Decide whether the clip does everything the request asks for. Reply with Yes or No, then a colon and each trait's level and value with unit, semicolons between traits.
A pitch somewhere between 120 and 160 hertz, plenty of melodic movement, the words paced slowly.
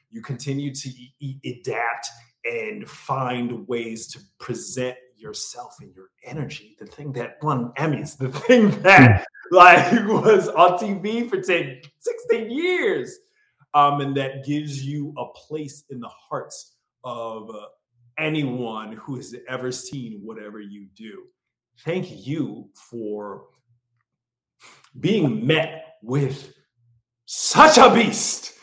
Yes: low, 135 Hz; wide, 5.9 semitones; slow, 125 wpm